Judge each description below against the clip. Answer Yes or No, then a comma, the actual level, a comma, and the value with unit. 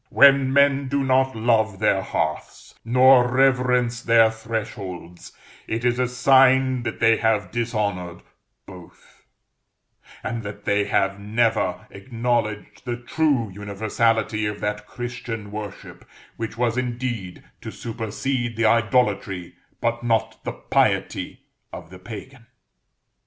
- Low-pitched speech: Yes, low, 115 Hz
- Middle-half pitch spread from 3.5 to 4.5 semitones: No, average, 3.1 semitones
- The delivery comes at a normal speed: No, slow, 120 wpm